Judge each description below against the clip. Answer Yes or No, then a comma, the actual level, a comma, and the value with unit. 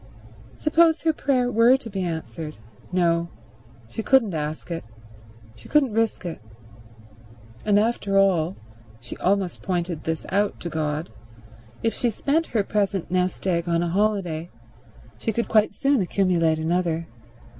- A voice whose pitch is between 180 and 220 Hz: Yes, medium, 185 Hz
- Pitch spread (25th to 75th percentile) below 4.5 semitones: No, average, 5.1 semitones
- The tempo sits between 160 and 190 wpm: No, slow, 135 wpm